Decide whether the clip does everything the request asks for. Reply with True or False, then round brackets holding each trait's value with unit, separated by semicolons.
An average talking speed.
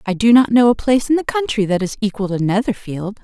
False (260 wpm)